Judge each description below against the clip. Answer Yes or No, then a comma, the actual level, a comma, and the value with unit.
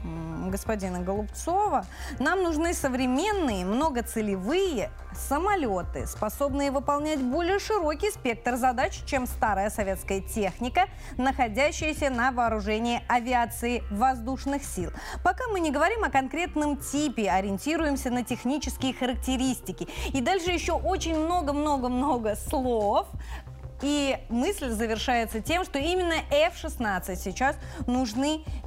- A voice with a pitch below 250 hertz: No, very high, 265 Hz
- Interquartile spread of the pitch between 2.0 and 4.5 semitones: No, wide, 5.4 semitones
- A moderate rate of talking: No, slow, 105 wpm